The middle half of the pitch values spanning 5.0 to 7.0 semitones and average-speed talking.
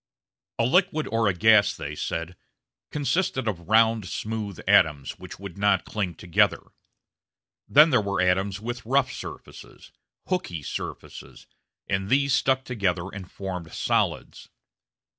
No: wide, 5.5 semitones; slow, 130 wpm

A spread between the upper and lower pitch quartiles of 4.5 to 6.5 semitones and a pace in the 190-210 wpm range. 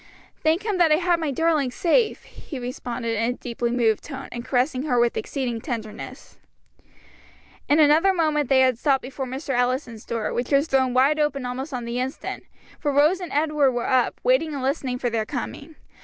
No: average, 3.6 semitones; average, 195 wpm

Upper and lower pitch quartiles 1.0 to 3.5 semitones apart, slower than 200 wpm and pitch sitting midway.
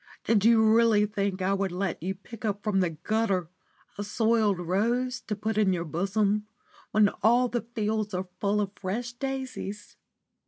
No: average, 2.8 semitones; average, 170 wpm; high, 210 Hz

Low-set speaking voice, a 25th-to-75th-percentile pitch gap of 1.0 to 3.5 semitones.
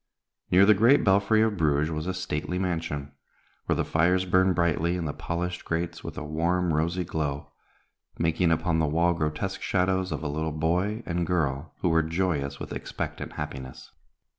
Yes: very low, 85 Hz; average, 2.9 semitones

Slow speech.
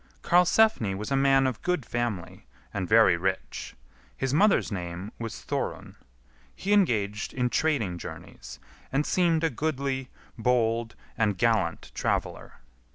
Yes: slow, 130 wpm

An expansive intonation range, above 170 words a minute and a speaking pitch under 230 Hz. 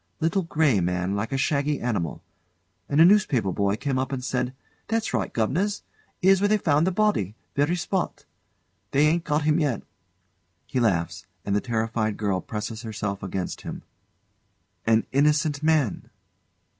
No: wide, 7.0 semitones; average, 155 wpm; low, 135 Hz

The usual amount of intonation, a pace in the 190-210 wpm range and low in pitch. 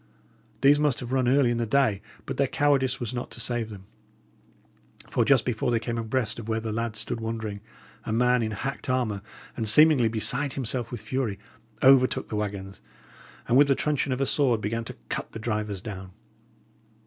Yes: average, 3.3 semitones; average, 195 wpm; low, 120 Hz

